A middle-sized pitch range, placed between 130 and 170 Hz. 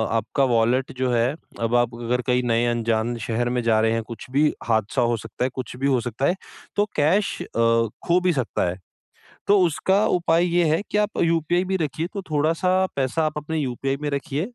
No: wide, 5.7 semitones; low, 135 Hz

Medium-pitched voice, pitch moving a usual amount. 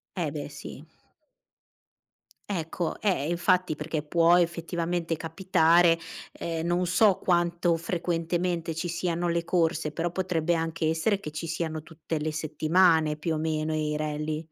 No: medium, 165 Hz; narrow, 1.8 semitones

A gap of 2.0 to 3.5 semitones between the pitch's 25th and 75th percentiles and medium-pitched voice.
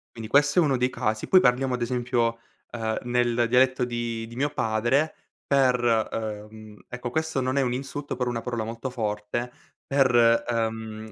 No: narrow, 2.4 semitones; low, 120 Hz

